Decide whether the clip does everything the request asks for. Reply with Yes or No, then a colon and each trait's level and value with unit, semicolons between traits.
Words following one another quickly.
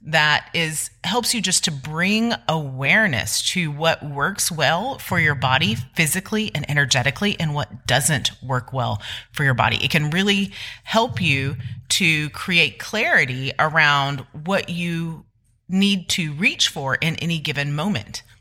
No: average, 145 wpm